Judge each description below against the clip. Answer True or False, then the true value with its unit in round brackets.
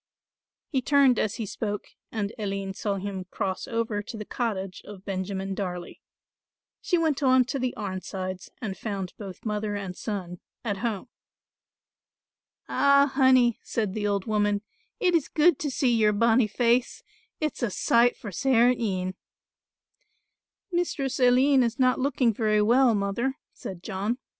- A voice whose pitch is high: True (220 Hz)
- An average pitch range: True (4.4 semitones)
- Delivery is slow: False (150 wpm)